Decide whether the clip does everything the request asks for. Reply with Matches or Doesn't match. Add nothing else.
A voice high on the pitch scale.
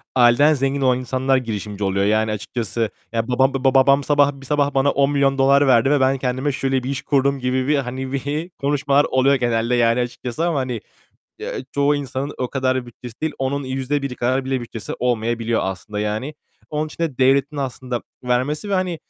Doesn't match